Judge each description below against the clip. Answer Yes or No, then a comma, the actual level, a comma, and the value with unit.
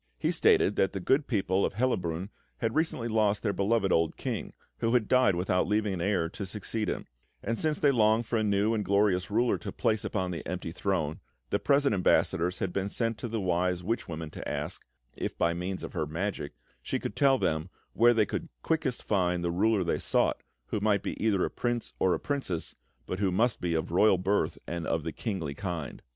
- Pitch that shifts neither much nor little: Yes, average, 4.0 semitones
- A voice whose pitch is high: No, low, 100 Hz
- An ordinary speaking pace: No, fast, 215 wpm